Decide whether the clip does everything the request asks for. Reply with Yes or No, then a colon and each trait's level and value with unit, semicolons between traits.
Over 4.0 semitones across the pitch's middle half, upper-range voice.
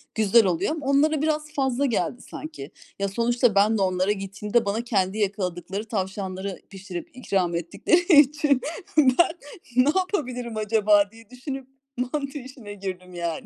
Yes: wide, 5.5 semitones; high, 220 Hz